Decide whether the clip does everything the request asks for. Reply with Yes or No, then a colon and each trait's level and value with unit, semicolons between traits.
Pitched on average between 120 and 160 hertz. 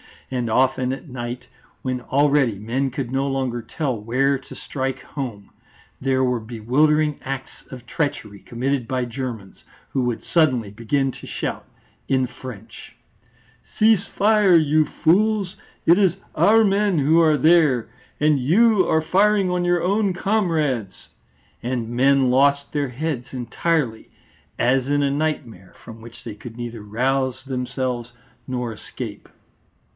Yes: low, 135 Hz